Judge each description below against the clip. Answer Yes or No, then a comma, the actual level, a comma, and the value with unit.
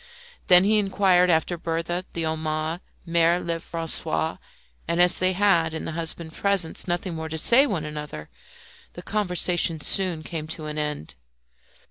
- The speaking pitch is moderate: Yes, medium, 170 Hz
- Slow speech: No, average, 155 wpm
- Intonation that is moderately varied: No, narrow, 2.1 semitones